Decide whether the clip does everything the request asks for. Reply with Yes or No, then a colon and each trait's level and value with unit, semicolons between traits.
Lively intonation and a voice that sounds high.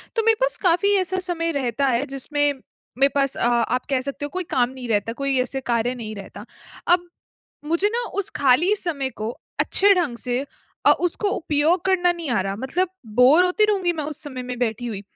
Yes: wide, 6.0 semitones; very high, 280 Hz